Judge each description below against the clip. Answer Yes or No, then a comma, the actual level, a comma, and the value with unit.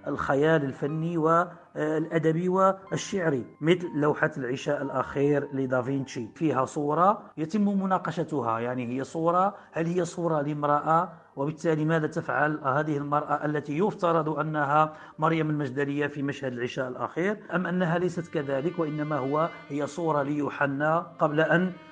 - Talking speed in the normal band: Yes, average, 125 wpm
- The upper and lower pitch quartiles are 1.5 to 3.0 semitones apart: Yes, average, 2.7 semitones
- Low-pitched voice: No, medium, 155 Hz